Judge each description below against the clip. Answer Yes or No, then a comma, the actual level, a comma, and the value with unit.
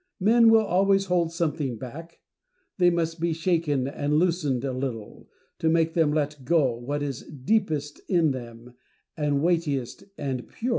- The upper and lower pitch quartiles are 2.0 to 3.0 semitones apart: No, average, 3.9 semitones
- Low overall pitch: No, medium, 155 Hz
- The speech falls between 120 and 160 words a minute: Yes, average, 155 wpm